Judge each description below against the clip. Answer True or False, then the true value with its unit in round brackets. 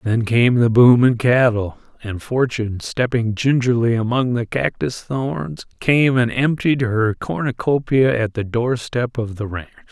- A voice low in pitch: True (120 Hz)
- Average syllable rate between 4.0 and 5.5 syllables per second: True (4.1 syllables/s)